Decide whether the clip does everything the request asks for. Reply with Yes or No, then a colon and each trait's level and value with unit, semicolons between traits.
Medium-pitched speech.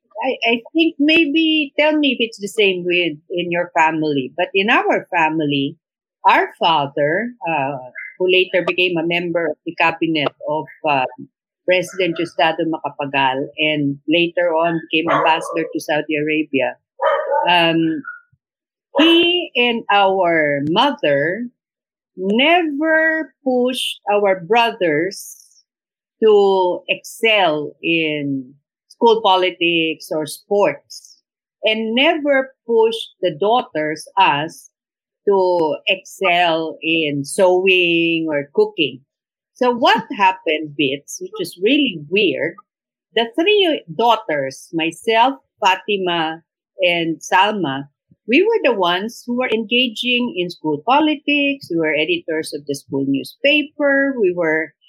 Yes: medium, 180 Hz